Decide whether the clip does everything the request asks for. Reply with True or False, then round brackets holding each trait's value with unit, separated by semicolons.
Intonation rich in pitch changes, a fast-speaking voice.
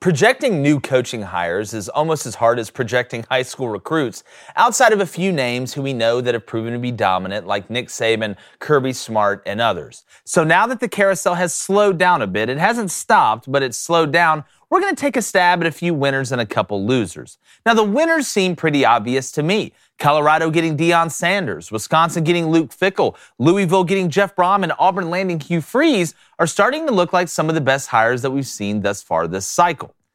True (6.9 semitones; 215 wpm)